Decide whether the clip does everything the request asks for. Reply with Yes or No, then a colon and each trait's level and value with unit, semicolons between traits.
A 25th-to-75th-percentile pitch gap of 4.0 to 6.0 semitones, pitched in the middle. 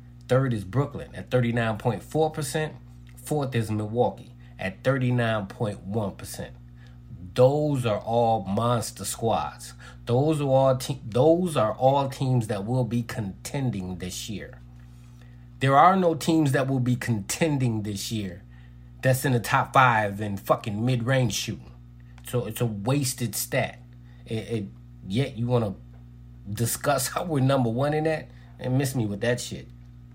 No: average, 4.9 semitones; low, 120 Hz